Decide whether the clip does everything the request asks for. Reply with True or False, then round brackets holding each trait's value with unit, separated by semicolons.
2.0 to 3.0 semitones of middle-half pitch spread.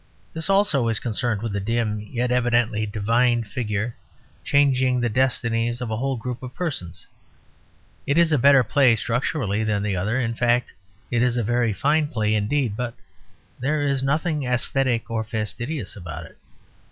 False (3.4 semitones)